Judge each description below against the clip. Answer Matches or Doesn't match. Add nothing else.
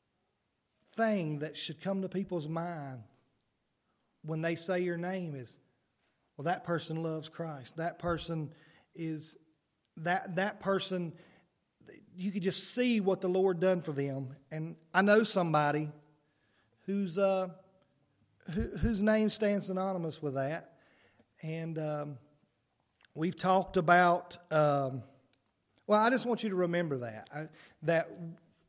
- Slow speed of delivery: Matches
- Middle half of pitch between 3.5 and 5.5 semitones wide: Matches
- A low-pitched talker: Doesn't match